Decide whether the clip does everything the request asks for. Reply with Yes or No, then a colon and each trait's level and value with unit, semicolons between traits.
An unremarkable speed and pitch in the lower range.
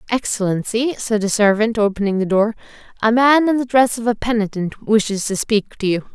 No: average, 195 wpm; high, 220 Hz